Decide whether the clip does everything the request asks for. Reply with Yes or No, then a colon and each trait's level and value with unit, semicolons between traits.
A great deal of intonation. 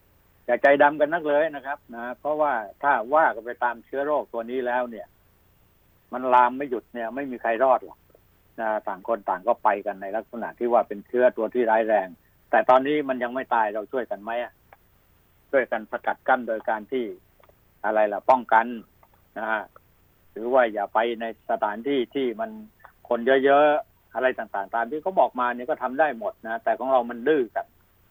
No: average, 3.6 semitones